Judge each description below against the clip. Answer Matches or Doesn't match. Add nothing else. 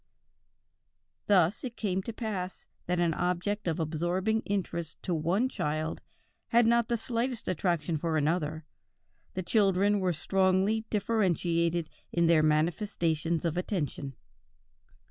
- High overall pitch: Doesn't match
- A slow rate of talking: Matches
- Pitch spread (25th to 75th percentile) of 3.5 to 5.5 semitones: Matches